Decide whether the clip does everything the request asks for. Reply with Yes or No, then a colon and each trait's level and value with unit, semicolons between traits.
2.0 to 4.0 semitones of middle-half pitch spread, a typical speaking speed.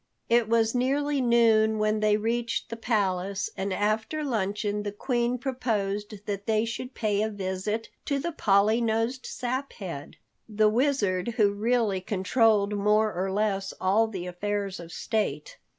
Yes: average, 2.8 semitones; average, 150 wpm